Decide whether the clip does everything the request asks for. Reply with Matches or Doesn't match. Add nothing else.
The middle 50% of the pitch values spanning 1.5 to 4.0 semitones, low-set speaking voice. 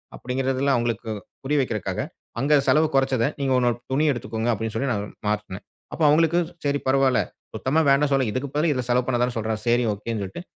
Matches